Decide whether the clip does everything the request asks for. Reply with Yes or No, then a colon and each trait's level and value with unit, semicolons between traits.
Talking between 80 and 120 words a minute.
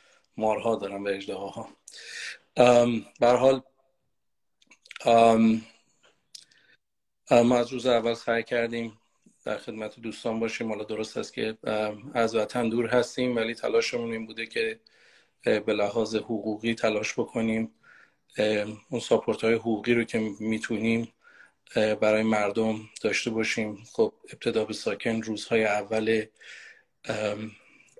Yes: average, 115 wpm